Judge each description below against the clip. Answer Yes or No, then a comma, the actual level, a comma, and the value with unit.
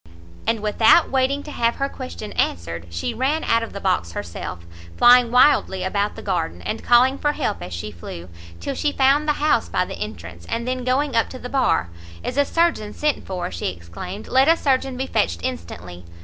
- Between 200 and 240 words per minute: Yes, fast, 205 wpm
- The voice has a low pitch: No, high, 225 Hz